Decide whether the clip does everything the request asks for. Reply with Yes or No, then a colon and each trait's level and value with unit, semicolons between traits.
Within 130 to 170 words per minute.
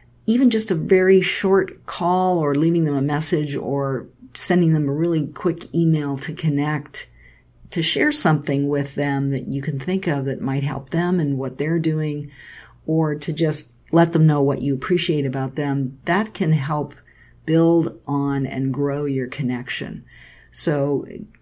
Yes: average, 165 wpm